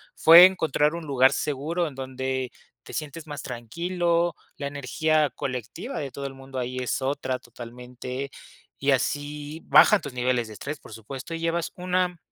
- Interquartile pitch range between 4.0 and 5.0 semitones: Yes, average, 4.3 semitones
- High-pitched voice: No, medium, 140 Hz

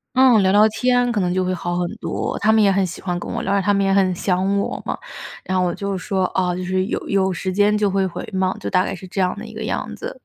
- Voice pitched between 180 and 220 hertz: Yes, high, 190 Hz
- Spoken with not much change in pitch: Yes, narrow, 1.8 semitones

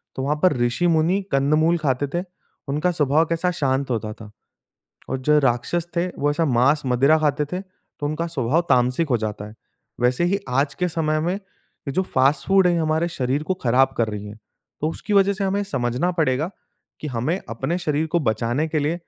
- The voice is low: No, medium, 150 Hz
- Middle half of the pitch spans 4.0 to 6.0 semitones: Yes, average, 4.8 semitones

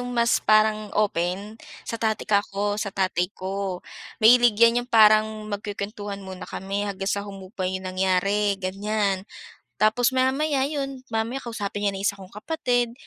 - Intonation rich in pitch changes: No, average, 2.9 semitones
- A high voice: Yes, high, 205 Hz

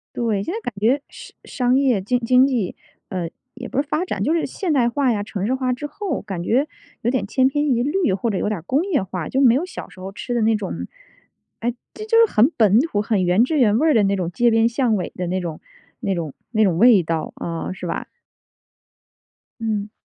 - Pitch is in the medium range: No, high, 230 Hz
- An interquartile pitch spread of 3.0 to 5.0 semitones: No, wide, 5.4 semitones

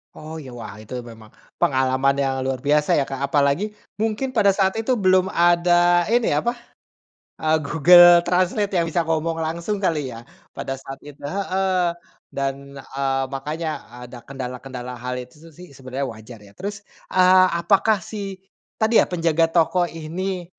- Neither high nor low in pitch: Yes, medium, 165 Hz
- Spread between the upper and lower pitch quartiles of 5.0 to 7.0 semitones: Yes, wide, 5.4 semitones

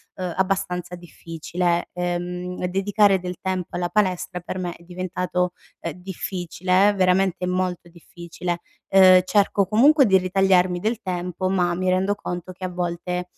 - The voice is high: No, medium, 180 Hz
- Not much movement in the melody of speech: Yes, narrow, 1.3 semitones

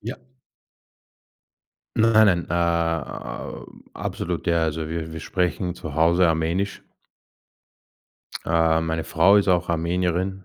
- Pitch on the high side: No, very low, 85 Hz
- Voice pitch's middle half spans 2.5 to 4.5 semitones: No, narrow, 2.0 semitones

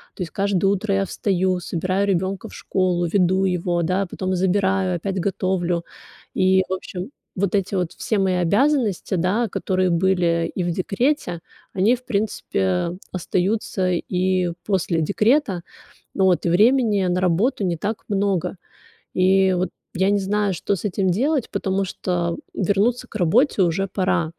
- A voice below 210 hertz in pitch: Yes, high, 190 Hz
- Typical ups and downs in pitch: No, narrow, 2.1 semitones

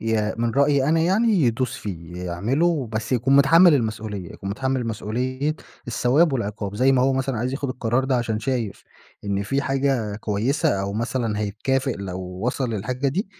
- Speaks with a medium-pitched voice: No, low, 125 Hz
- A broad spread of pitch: No, average, 4.2 semitones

